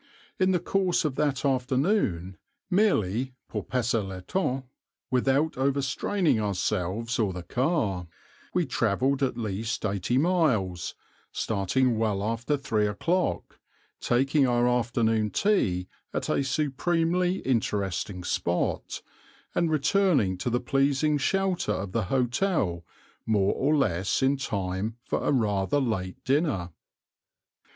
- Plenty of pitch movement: Yes, wide, 6.3 semitones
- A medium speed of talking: No, slow, 120 wpm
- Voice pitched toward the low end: Yes, low, 125 Hz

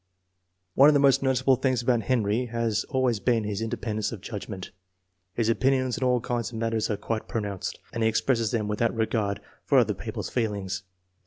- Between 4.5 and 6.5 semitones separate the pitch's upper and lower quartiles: No, average, 2.9 semitones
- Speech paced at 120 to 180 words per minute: No, average, 190 wpm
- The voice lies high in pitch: No, low, 115 Hz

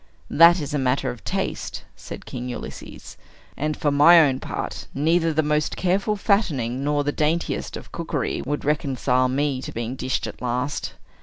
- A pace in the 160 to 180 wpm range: Yes, average, 170 wpm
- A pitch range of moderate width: Yes, average, 3.6 semitones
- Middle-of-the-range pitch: Yes, medium, 145 Hz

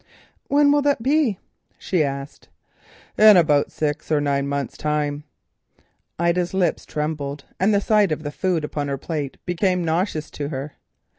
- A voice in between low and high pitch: Yes, medium, 155 Hz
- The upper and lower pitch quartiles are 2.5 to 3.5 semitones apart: No, average, 4.6 semitones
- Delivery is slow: No, average, 155 wpm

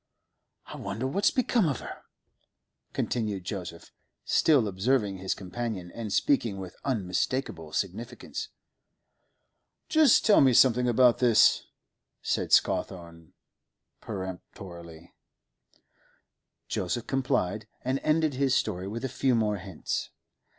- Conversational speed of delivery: No, slow, 110 wpm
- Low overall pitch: Yes, low, 110 Hz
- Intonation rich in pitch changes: Yes, wide, 5.8 semitones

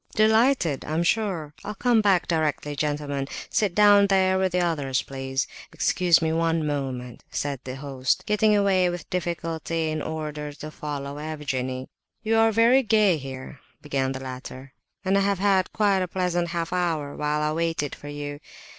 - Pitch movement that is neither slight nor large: Yes, average, 4.7 semitones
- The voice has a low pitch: No, medium, 160 Hz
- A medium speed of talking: Yes, average, 160 wpm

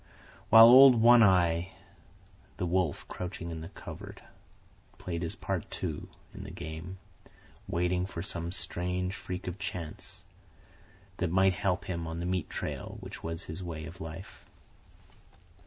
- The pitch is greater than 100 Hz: No, very low, 90 Hz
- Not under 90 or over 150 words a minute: Yes, average, 145 wpm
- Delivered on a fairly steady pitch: Yes, narrow, 2.1 semitones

